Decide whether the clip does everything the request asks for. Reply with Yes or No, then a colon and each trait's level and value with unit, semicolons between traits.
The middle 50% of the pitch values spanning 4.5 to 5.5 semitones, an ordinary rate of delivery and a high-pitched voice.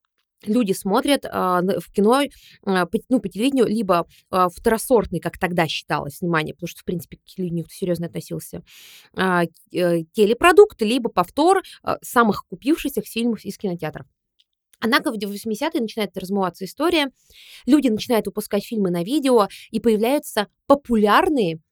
Yes: average, 5.1 semitones; average, 140 wpm; high, 210 Hz